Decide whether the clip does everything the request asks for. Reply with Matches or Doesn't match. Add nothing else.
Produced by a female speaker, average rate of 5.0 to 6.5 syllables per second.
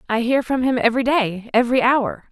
Matches